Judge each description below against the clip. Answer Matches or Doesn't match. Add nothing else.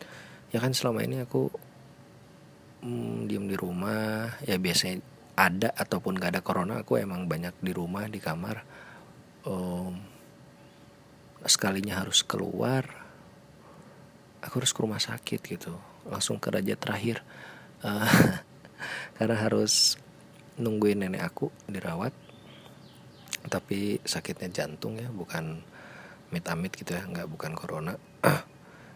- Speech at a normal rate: Matches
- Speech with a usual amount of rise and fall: Matches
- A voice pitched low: Matches